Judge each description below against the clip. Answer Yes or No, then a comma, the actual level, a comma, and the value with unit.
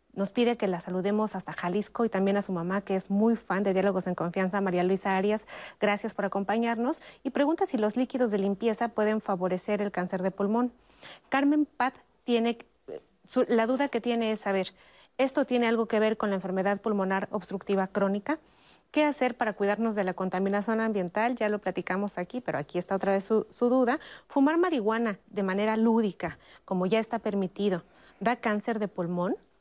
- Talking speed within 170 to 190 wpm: Yes, average, 185 wpm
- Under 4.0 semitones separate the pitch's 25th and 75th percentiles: Yes, average, 3.4 semitones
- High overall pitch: Yes, high, 210 Hz